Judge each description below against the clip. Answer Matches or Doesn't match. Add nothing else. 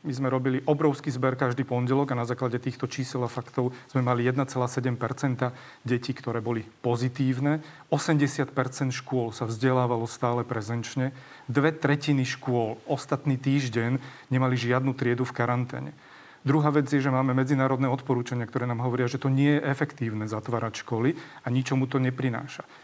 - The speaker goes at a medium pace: Matches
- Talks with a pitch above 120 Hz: Matches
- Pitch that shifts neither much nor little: Doesn't match